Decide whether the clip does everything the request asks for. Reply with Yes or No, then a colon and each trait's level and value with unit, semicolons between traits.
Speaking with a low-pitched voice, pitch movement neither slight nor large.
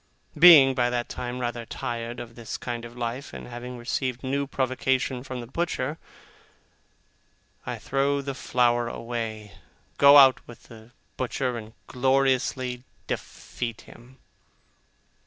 No: low, 125 Hz; narrow, 1.9 semitones